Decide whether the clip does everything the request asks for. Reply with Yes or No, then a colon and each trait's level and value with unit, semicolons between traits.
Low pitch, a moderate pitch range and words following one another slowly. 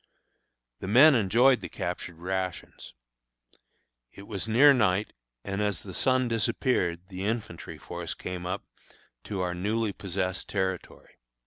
Yes: low, 100 Hz; average, 3.7 semitones; slow, 130 wpm